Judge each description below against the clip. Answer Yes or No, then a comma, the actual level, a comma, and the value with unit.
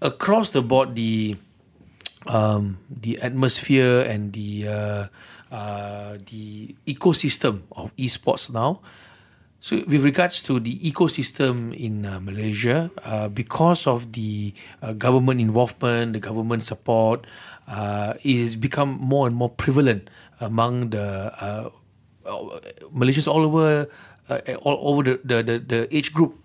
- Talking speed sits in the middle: No, slow, 130 wpm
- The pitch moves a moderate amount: Yes, average, 4.6 semitones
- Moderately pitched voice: No, low, 120 Hz